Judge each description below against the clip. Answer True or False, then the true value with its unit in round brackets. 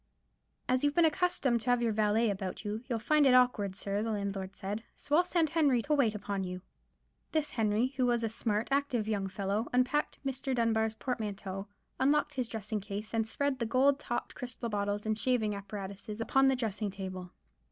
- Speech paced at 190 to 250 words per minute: True (195 wpm)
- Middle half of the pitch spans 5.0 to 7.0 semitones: False (4.2 semitones)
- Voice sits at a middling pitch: False (225 Hz)